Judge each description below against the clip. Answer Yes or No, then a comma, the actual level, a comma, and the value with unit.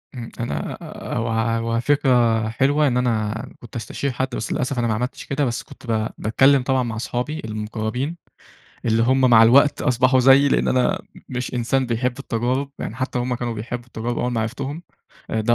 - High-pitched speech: No, low, 120 Hz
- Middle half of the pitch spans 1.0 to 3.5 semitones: Yes, narrow, 2.5 semitones